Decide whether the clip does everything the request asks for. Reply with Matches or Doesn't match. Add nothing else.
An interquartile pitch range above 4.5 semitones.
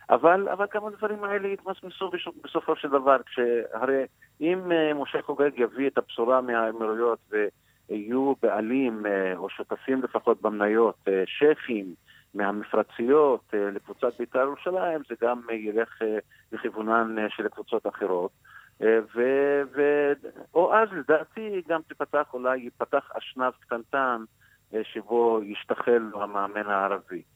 Matches